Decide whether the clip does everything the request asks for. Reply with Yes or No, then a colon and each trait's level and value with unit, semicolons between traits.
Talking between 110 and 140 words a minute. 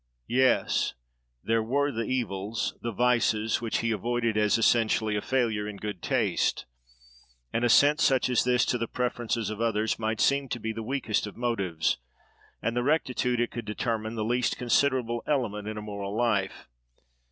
No: average, 170 wpm